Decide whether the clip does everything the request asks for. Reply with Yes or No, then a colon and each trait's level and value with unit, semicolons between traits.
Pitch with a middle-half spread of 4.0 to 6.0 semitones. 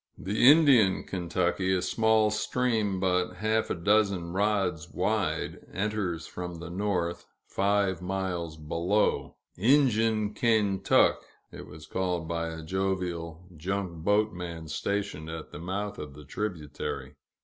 No: average, 3.6 semitones